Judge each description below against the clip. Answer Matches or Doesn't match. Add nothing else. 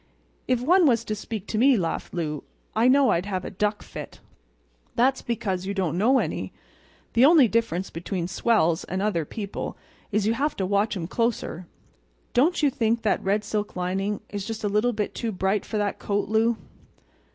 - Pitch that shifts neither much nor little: Matches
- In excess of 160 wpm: Matches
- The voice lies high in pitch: Matches